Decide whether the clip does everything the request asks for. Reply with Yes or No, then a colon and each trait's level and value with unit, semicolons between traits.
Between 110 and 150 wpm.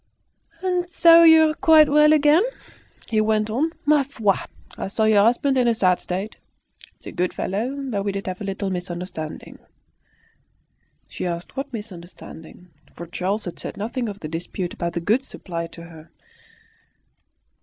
No: average, 165 wpm